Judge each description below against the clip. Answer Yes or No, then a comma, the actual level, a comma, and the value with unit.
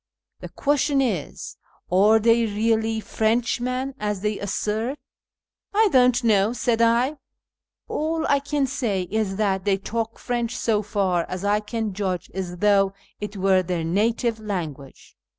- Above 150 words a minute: Yes, average, 160 wpm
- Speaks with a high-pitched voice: Yes, high, 215 Hz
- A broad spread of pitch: No, average, 3.5 semitones